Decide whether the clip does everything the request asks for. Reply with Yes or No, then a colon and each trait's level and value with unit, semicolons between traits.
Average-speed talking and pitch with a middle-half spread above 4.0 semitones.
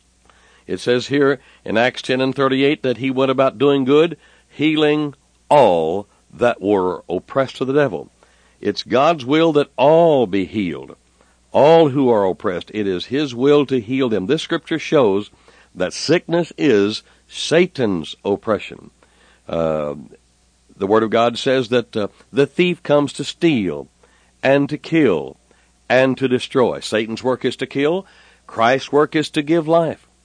Yes: average, 155 wpm; average, 5.2 semitones